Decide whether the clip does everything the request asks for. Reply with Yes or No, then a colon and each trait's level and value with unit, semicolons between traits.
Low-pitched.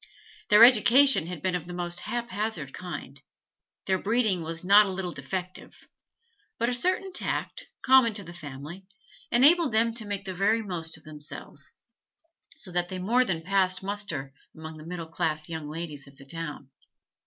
No: medium, 185 Hz